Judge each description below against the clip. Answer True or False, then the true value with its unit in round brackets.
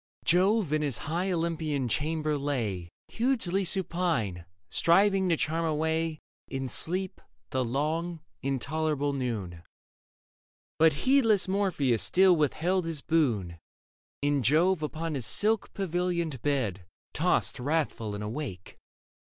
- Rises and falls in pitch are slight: False (4.9 semitones)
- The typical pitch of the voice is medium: True (155 Hz)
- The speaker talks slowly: True (115 wpm)